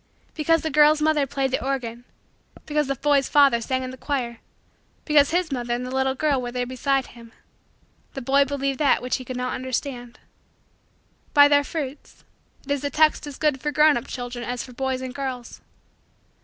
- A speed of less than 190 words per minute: No, average, 195 wpm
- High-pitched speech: Yes, very high, 270 Hz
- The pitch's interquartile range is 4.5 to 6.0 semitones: No, narrow, 2.5 semitones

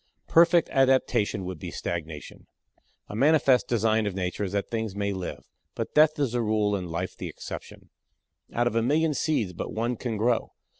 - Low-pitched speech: Yes, low, 110 Hz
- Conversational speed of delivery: Yes, average, 185 wpm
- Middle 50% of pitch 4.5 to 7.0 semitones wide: Yes, average, 4.9 semitones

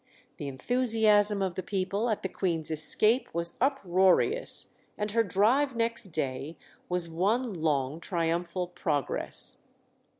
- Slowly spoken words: Yes, slow, 125 wpm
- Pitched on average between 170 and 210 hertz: Yes, high, 190 Hz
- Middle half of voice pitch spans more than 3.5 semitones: Yes, average, 5.0 semitones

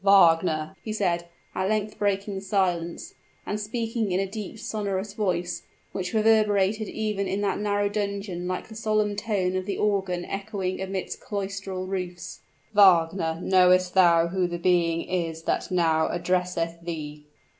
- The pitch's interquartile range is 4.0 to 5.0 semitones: No, narrow, 2.6 semitones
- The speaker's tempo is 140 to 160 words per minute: Yes, average, 145 wpm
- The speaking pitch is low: No, high, 190 Hz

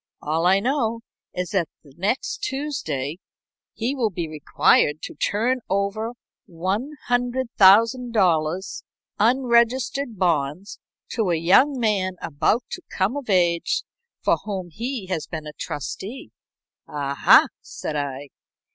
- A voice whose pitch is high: Yes, high, 195 Hz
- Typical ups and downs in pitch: No, wide, 6.4 semitones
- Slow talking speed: Yes, slow, 115 wpm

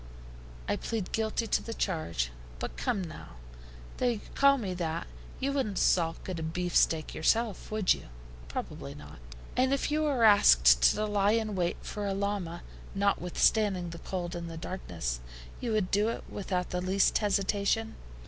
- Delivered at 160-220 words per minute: Yes, average, 165 wpm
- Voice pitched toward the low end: No, high, 195 Hz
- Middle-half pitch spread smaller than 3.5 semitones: No, average, 4.2 semitones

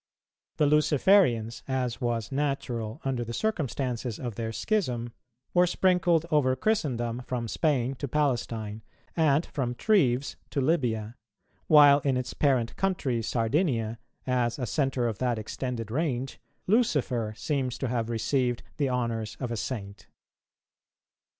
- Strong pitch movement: No, average, 3.9 semitones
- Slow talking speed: Yes, slow, 130 wpm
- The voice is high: No, low, 125 Hz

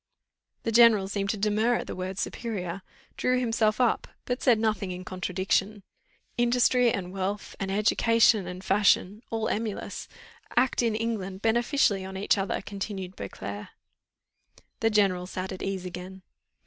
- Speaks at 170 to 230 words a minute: No, average, 150 wpm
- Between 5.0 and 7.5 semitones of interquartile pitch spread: No, average, 3.2 semitones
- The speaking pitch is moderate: No, high, 200 Hz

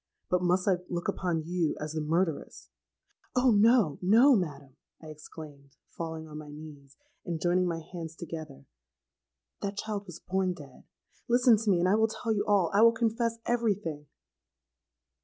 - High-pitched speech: No, medium, 175 Hz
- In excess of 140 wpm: Yes, average, 165 wpm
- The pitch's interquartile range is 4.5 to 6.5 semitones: Yes, average, 4.9 semitones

